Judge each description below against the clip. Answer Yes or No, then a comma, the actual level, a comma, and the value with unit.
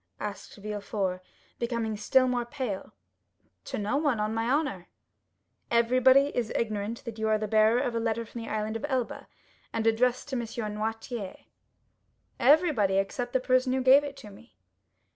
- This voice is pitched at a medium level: No, high, 230 Hz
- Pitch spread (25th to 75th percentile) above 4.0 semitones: No, average, 3.0 semitones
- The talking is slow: No, average, 165 wpm